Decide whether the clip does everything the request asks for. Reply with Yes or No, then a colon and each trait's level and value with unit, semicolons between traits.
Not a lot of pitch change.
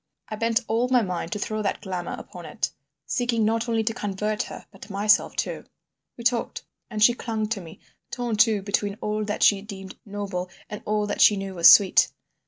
Yes: narrow, 2.2 semitones